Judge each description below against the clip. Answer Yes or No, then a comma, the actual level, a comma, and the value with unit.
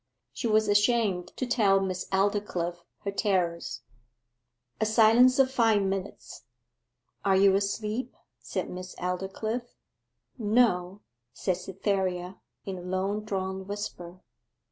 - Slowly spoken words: Yes, slow, 115 wpm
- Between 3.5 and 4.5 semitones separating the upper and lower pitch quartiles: No, average, 2.7 semitones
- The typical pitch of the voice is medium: No, high, 195 Hz